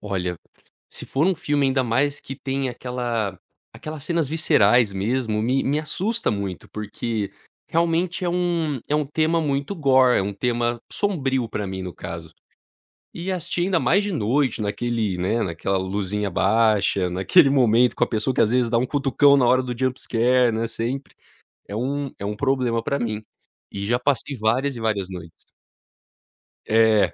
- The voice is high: No, low, 125 Hz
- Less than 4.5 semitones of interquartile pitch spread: No, average, 5.1 semitones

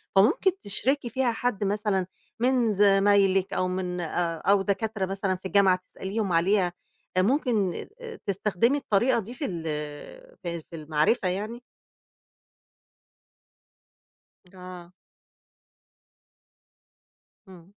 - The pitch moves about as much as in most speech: Yes, average, 3.4 semitones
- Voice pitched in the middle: No, high, 195 Hz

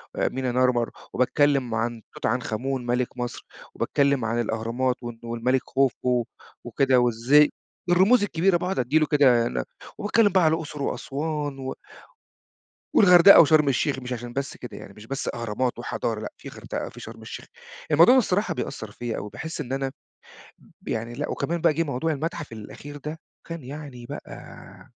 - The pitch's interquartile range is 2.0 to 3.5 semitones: No, average, 4.3 semitones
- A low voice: Yes, low, 130 Hz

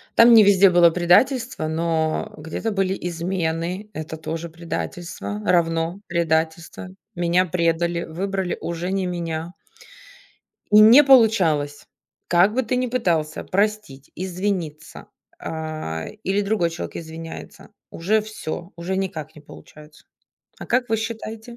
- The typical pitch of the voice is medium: Yes, medium, 175 Hz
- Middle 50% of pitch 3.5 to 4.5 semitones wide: Yes, average, 3.9 semitones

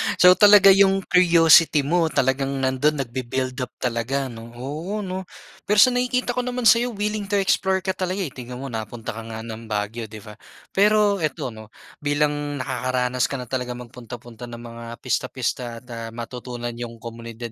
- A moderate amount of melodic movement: No, wide, 8.0 semitones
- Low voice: Yes, low, 130 Hz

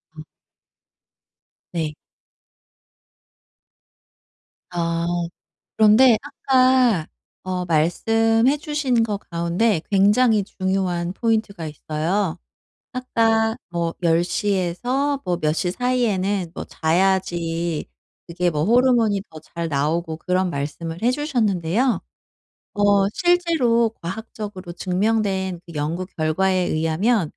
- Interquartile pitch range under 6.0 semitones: Yes, average, 5.1 semitones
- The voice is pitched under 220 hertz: Yes, high, 190 Hz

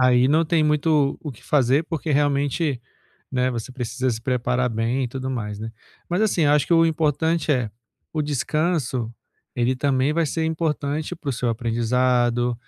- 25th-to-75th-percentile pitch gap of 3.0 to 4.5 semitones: Yes, average, 3.8 semitones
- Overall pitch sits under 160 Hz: Yes, low, 135 Hz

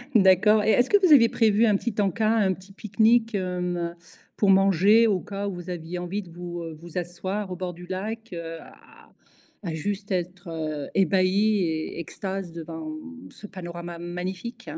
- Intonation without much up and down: No, average, 3.1 semitones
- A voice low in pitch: No, medium, 185 Hz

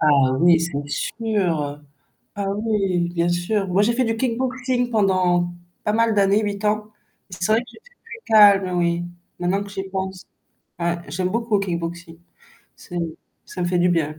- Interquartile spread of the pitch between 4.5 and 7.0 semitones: No, average, 3.7 semitones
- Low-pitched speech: No, high, 190 Hz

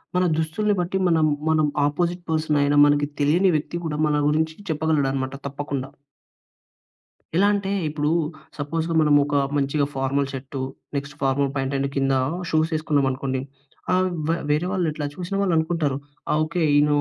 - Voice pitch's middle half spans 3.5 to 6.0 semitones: No, average, 2.7 semitones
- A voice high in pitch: No, medium, 150 Hz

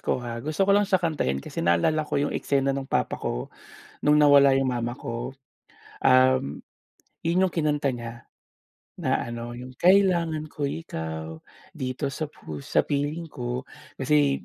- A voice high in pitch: No, low, 135 Hz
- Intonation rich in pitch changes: No, average, 4.4 semitones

